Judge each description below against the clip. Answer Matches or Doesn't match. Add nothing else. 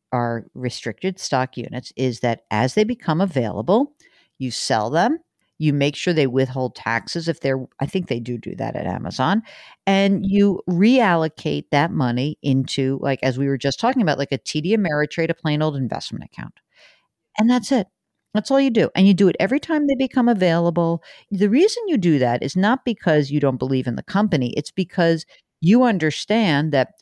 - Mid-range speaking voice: Matches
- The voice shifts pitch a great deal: Matches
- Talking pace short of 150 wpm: Doesn't match